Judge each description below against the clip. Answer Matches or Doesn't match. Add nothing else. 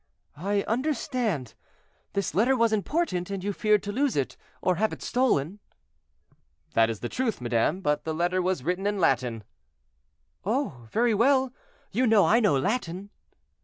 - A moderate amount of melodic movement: Doesn't match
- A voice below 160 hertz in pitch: Doesn't match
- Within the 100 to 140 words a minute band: Doesn't match